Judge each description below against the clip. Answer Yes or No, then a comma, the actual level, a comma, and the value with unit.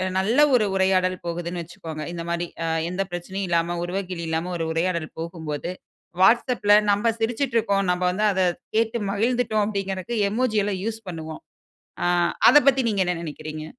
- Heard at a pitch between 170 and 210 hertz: Yes, high, 190 Hz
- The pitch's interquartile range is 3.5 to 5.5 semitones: Yes, average, 4.1 semitones